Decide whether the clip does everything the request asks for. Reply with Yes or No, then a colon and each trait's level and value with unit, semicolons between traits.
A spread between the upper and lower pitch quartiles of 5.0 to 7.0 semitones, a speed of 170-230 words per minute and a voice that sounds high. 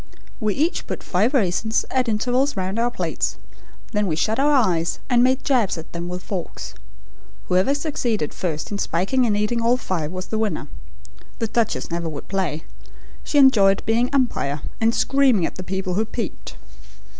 Yes: average, 5.3 semitones; average, 175 wpm; high, 215 Hz